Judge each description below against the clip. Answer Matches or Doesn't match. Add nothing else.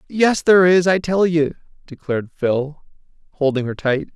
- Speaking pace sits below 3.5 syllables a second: Doesn't match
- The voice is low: Doesn't match